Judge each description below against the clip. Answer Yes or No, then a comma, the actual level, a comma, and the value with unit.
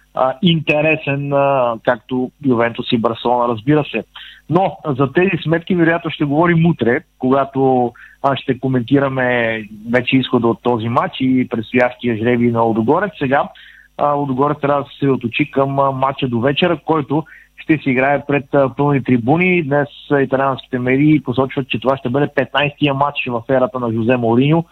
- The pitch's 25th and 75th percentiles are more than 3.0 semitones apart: No, average, 2.7 semitones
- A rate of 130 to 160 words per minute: Yes, average, 150 wpm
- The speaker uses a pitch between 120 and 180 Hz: Yes, low, 135 Hz